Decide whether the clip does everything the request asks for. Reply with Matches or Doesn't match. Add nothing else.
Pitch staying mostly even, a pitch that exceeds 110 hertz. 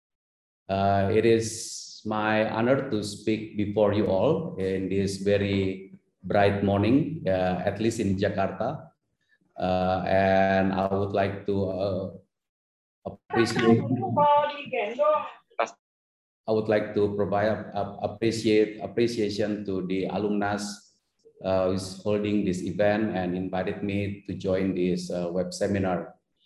Doesn't match